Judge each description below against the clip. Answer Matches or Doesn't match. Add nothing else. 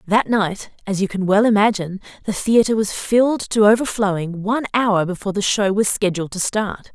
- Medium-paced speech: Matches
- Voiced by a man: Doesn't match